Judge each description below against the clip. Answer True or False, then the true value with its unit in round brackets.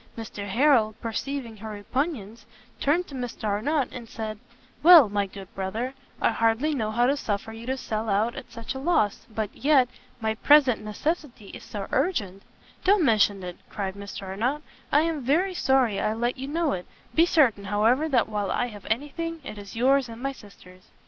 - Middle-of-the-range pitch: False (230 Hz)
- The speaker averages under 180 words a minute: False (190 wpm)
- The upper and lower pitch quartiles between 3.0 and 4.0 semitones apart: False (5.1 semitones)